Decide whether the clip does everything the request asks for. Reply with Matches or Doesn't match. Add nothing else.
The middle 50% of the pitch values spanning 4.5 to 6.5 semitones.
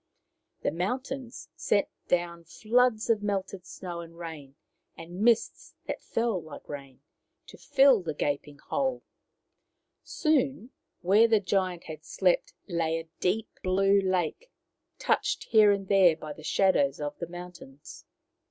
Matches